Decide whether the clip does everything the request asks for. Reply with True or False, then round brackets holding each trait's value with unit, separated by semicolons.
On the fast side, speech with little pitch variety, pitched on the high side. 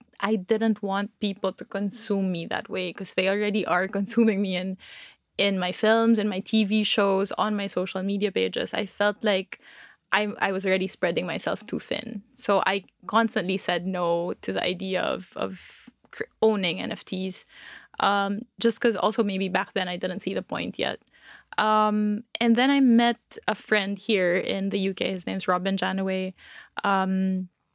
False (175 wpm; 2.2 semitones; 200 Hz)